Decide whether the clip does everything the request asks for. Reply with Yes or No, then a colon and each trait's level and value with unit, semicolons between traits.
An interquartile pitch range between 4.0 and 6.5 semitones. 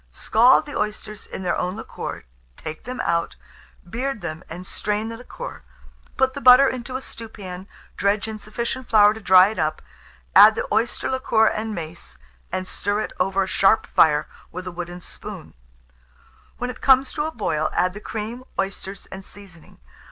Yes: average, 4.4 semitones